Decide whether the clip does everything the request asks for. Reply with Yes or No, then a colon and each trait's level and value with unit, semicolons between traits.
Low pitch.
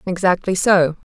No: medium, 180 Hz